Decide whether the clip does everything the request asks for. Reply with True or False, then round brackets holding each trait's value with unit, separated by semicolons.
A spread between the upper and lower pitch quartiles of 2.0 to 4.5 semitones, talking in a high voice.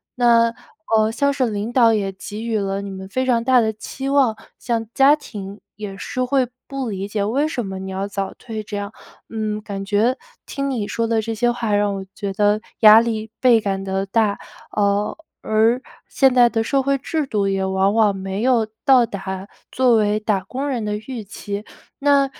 True (3.5 semitones; 220 Hz)